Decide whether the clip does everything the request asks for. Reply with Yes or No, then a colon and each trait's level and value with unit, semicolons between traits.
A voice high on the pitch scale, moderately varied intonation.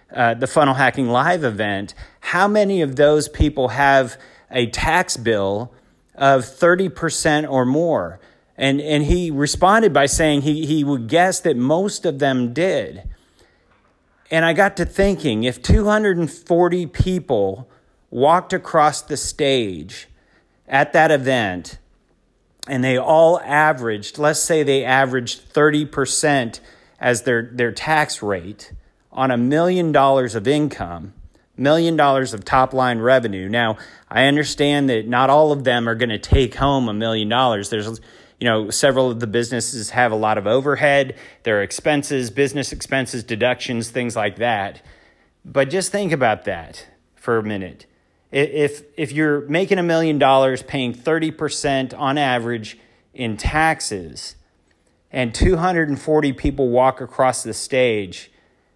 No: low, 135 Hz; average, 4.3 semitones